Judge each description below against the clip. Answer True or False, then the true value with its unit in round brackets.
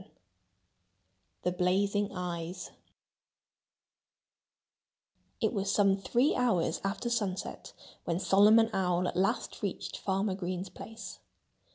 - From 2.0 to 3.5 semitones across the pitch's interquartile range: True (2.4 semitones)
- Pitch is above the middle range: True (195 Hz)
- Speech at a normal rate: False (100 wpm)